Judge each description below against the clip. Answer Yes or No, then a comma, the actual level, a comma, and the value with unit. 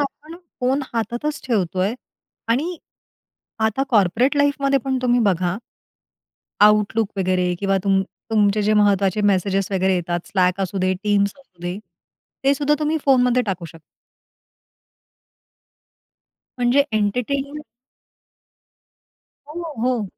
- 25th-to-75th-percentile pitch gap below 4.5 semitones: No, wide, 5.6 semitones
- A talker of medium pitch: No, high, 210 Hz